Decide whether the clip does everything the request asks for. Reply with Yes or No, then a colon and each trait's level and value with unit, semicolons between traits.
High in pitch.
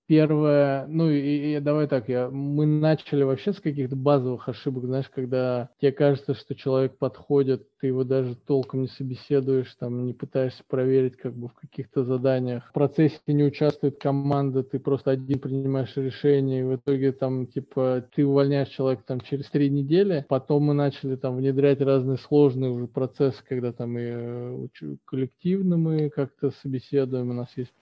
No: low, 135 Hz